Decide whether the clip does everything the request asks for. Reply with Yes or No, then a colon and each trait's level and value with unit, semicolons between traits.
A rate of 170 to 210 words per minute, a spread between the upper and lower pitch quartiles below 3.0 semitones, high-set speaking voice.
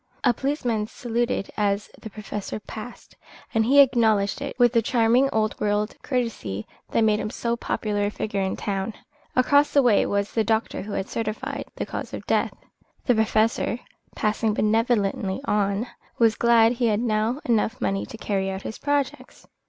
Yes: average, 175 wpm; narrow, 2.5 semitones; high, 220 Hz